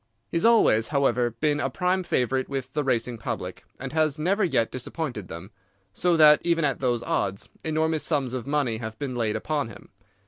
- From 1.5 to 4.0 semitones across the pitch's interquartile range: No, average, 4.7 semitones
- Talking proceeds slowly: No, average, 195 wpm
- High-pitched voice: No, low, 135 Hz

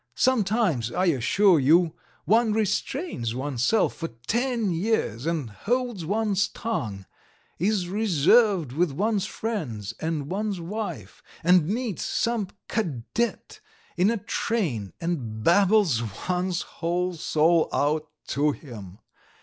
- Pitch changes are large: Yes, wide, 6.8 semitones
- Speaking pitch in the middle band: Yes, medium, 180 Hz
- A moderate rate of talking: No, slow, 115 wpm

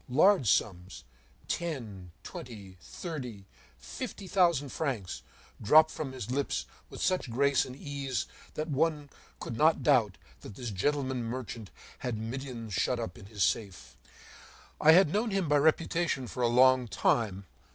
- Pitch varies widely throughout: Yes, wide, 5.8 semitones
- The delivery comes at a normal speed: Yes, average, 145 wpm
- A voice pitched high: No, low, 130 Hz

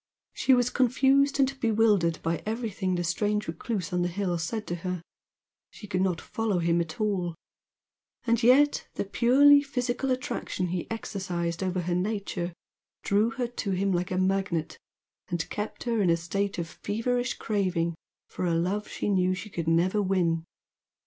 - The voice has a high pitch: Yes, high, 195 Hz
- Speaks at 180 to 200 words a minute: No, average, 170 wpm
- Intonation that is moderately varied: Yes, average, 4.5 semitones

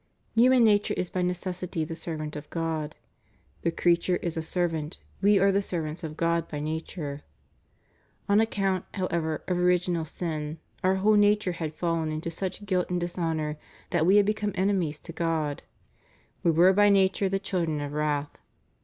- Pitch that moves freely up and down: No, average, 3.2 semitones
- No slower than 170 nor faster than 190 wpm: Yes, average, 175 wpm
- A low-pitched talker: No, medium, 175 Hz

